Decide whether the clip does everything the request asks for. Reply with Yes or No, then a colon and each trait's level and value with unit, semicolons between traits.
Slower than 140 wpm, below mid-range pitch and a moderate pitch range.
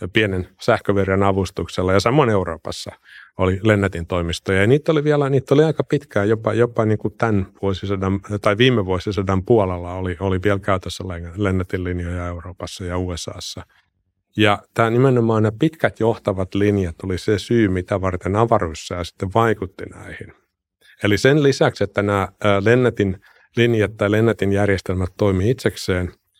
No: average, 145 wpm; low, 100 Hz; average, 3.4 semitones